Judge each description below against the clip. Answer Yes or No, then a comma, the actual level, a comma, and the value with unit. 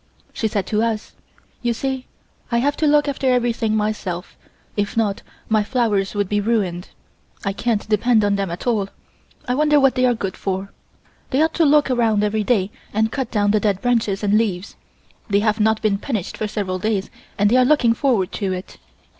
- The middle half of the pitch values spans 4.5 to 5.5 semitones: No, average, 3.3 semitones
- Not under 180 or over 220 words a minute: Yes, average, 200 wpm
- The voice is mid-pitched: No, high, 215 Hz